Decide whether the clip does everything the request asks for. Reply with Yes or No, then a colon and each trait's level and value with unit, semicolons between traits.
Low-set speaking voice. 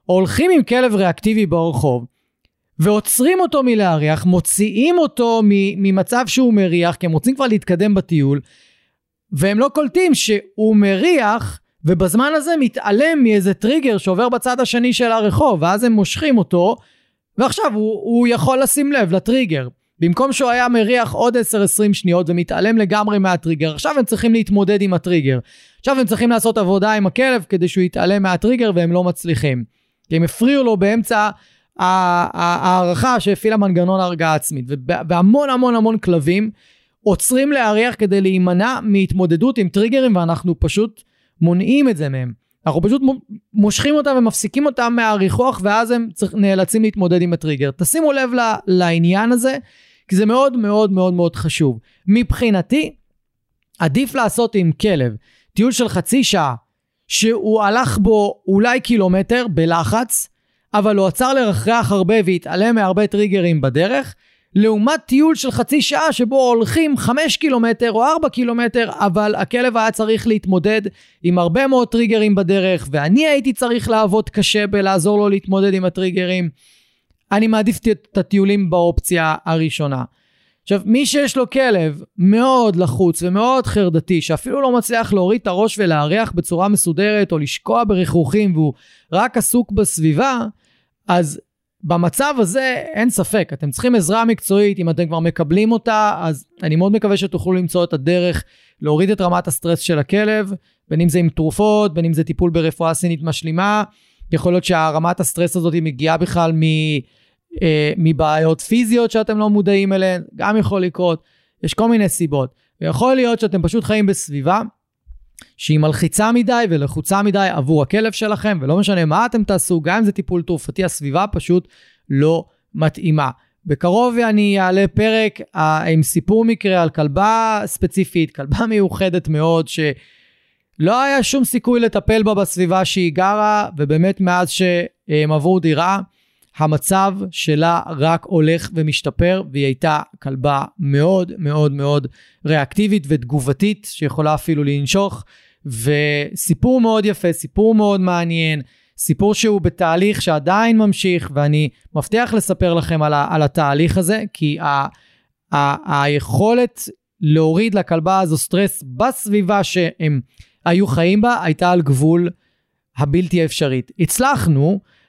No: high, 195 Hz